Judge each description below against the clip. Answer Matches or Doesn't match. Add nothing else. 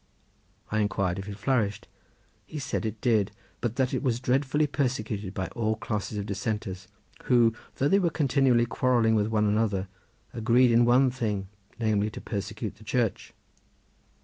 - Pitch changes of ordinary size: Matches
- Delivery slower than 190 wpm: Matches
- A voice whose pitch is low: Matches